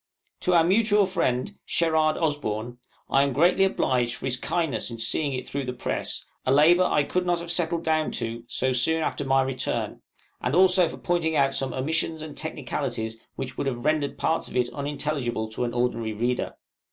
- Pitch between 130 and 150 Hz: Yes, medium, 140 Hz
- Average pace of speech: Yes, average, 190 wpm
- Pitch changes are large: No, average, 4.7 semitones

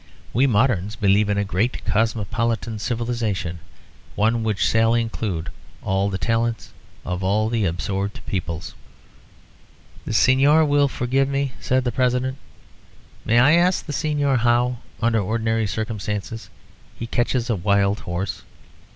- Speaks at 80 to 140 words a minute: Yes, slow, 135 wpm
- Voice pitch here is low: Yes, low, 115 Hz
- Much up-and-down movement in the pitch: No, average, 3.5 semitones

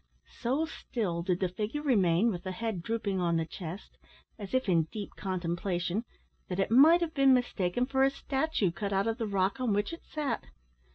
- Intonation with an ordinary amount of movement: No, wide, 5.9 semitones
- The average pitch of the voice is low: No, high, 205 Hz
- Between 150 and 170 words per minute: No, average, 195 wpm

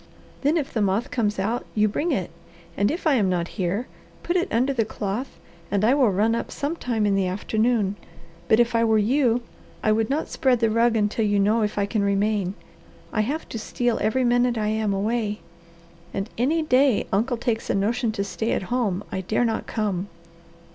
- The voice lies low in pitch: No, high, 220 Hz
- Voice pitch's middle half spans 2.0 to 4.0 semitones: Yes, average, 3.1 semitones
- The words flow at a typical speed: No, fast, 210 wpm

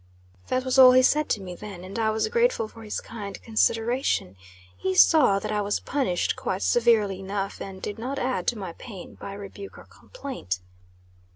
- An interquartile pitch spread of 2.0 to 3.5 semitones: No, average, 4.4 semitones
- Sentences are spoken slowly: No, average, 190 wpm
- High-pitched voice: Yes, high, 215 Hz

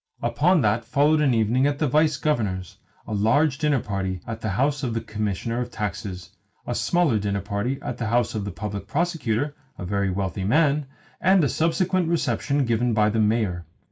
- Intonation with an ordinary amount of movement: No, wide, 6.0 semitones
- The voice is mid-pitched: No, low, 115 Hz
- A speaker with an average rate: Yes, average, 190 wpm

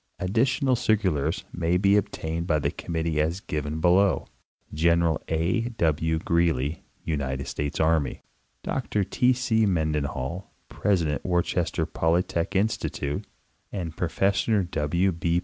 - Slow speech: Yes, slow, 120 wpm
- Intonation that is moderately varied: Yes, average, 3.7 semitones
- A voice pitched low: Yes, very low, 85 Hz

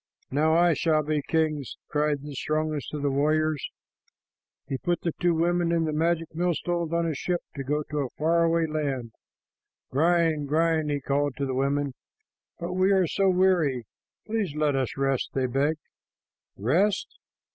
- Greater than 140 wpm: Yes, average, 170 wpm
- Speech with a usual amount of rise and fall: Yes, average, 3.0 semitones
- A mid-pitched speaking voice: Yes, medium, 155 Hz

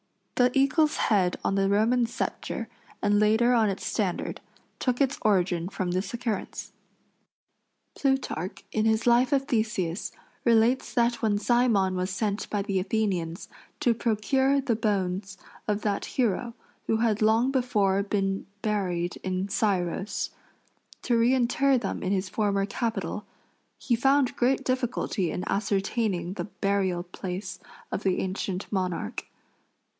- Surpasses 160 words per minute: No, slow, 135 wpm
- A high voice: Yes, high, 210 Hz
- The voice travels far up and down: No, average, 3.9 semitones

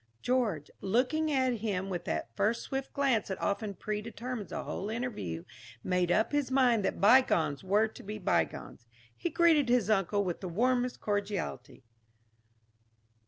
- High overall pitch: Yes, high, 215 Hz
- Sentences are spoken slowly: No, average, 150 wpm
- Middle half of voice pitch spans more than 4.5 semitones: Yes, average, 4.9 semitones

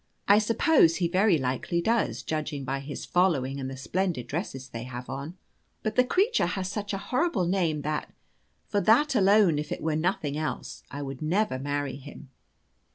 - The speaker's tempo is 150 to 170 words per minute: No, average, 185 wpm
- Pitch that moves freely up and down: Yes, wide, 6.3 semitones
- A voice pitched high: No, medium, 165 Hz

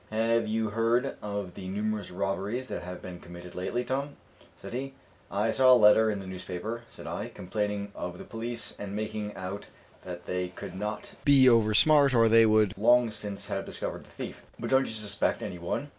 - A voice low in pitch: Yes, low, 110 Hz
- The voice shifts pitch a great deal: No, average, 3.1 semitones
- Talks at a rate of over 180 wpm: Yes, average, 200 wpm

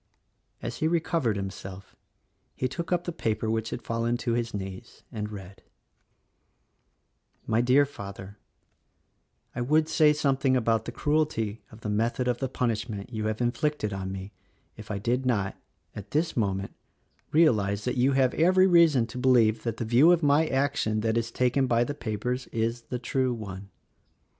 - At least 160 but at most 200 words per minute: Yes, average, 170 wpm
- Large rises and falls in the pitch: No, average, 4.2 semitones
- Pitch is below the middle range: Yes, low, 120 Hz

